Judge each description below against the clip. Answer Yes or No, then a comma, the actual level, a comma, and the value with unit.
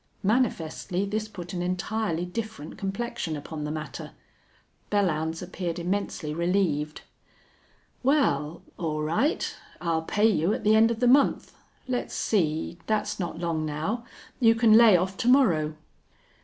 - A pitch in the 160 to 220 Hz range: Yes, medium, 185 Hz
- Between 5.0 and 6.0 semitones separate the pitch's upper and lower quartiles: Yes, average, 5.3 semitones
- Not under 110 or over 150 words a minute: Yes, average, 140 wpm